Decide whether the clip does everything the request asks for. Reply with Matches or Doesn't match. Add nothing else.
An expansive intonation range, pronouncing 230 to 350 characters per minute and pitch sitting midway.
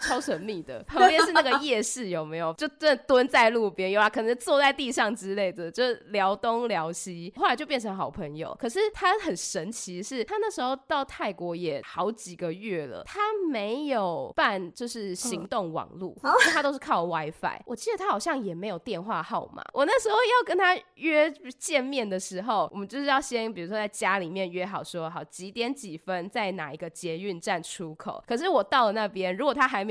Doesn't match